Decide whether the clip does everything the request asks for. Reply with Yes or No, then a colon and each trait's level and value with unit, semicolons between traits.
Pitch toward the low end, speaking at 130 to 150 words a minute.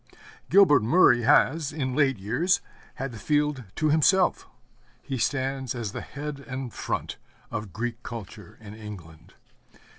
Yes: low, 130 Hz; average, 140 wpm